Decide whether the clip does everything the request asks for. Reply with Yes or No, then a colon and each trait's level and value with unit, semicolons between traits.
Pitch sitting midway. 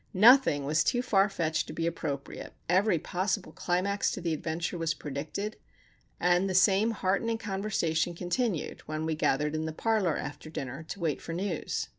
Yes: medium, 175 Hz